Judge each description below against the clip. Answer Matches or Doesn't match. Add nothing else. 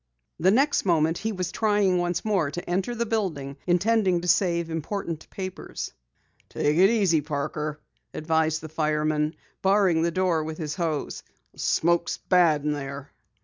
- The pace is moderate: Matches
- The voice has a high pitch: Doesn't match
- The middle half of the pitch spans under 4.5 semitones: Matches